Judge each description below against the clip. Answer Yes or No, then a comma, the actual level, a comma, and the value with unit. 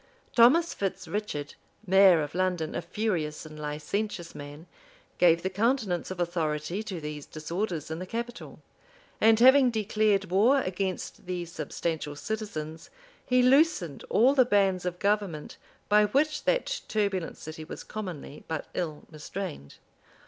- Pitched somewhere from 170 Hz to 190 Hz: Yes, medium, 185 Hz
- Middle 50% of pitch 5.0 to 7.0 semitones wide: Yes, average, 5.3 semitones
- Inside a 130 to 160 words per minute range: Yes, average, 140 wpm